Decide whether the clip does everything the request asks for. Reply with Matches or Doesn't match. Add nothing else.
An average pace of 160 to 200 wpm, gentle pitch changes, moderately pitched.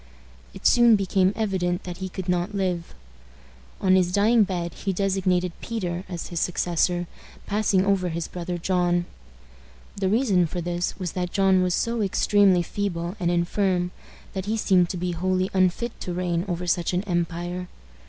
Matches